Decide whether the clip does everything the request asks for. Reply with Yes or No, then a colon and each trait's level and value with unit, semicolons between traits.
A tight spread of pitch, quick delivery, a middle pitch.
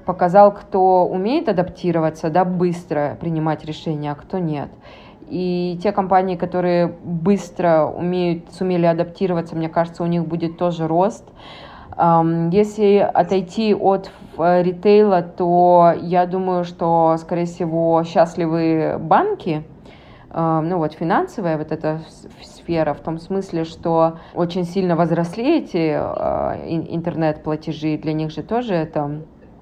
No: narrow, 2.3 semitones; average, 120 wpm; medium, 175 Hz